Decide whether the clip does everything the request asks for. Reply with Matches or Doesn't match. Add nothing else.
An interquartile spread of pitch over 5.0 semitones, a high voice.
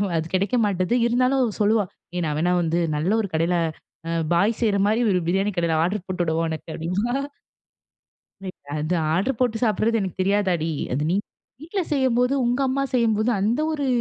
Matches